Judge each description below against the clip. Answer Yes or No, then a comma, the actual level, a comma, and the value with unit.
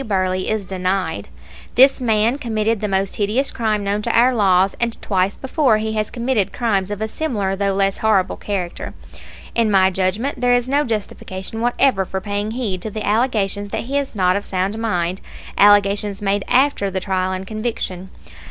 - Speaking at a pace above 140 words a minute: Yes, average, 180 wpm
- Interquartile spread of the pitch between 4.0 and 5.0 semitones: No, average, 3.1 semitones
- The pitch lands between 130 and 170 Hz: No, high, 205 Hz